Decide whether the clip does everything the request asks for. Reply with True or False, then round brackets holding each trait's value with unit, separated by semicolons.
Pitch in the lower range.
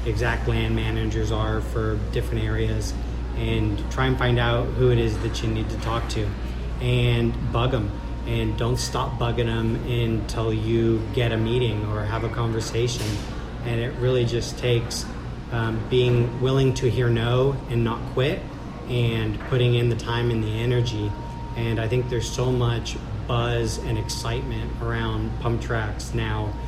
True (115 Hz)